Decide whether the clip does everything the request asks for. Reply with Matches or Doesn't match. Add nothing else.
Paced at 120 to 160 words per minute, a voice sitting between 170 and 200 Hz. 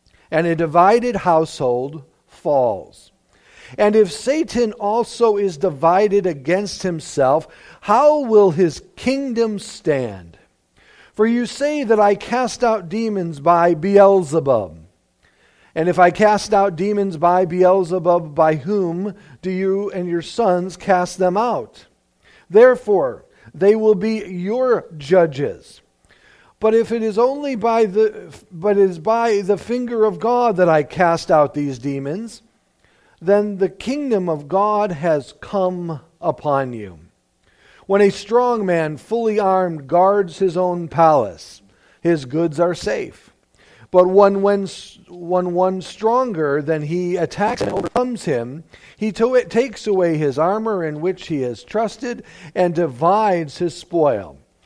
Matches